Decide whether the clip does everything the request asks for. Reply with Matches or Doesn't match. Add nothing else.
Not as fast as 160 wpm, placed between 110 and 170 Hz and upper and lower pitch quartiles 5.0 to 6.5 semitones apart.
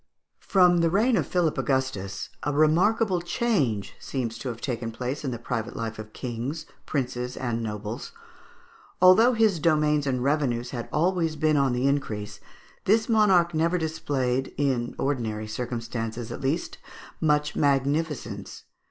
Matches